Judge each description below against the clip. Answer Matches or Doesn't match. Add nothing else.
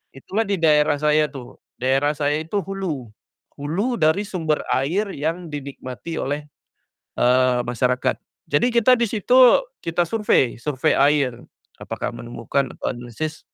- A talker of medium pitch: Matches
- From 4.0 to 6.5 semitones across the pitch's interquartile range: Matches